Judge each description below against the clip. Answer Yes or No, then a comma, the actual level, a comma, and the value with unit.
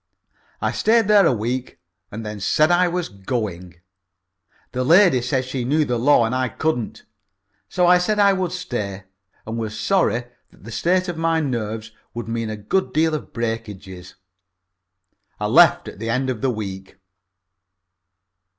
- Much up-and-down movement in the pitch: Yes, wide, 7.2 semitones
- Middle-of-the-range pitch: No, low, 125 Hz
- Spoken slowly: No, average, 165 wpm